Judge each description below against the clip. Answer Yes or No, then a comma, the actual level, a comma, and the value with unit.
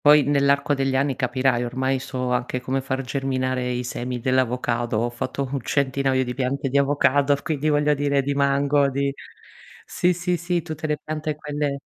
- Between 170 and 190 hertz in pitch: No, medium, 140 Hz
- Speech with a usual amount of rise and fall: No, narrow, 2.0 semitones